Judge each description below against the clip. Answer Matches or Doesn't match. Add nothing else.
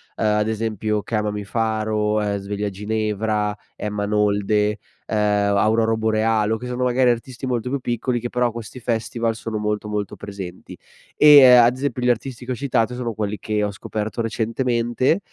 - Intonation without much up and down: Matches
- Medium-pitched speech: Doesn't match